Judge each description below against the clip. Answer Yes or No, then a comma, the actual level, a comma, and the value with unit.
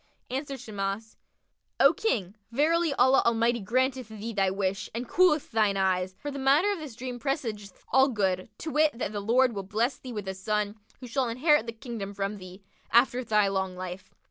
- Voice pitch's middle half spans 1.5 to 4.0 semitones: No, average, 5.0 semitones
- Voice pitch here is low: No, high, 230 Hz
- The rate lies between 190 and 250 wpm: Yes, average, 195 wpm